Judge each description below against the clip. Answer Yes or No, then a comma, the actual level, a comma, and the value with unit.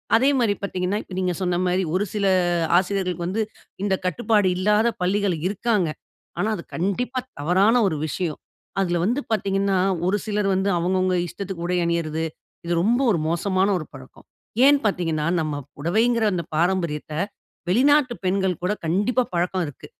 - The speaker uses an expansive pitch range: No, average, 3.1 semitones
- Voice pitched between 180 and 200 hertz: Yes, high, 190 Hz